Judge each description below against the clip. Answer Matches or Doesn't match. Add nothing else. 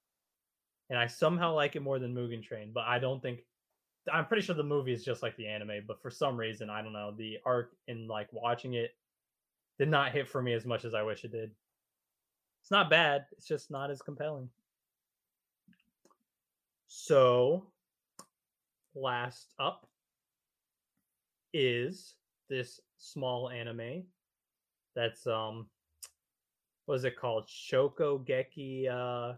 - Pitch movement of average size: Matches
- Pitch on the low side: Matches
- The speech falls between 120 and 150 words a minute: Matches